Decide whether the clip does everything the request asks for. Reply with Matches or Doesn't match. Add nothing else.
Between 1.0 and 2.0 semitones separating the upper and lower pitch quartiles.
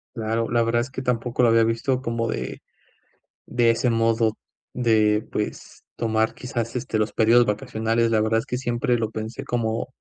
Matches